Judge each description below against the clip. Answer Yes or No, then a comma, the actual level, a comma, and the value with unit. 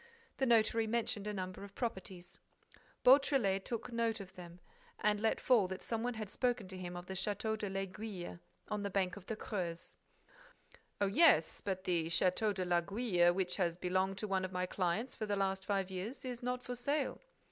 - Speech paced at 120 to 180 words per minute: No, average, 195 wpm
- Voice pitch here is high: Yes, high, 195 Hz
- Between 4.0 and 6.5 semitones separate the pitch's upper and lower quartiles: No, average, 3.4 semitones